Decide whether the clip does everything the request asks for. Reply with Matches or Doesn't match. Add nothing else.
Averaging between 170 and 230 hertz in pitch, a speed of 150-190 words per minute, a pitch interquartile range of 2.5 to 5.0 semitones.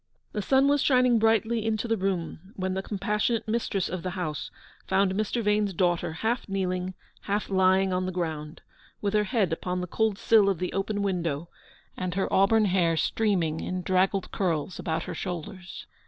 Matches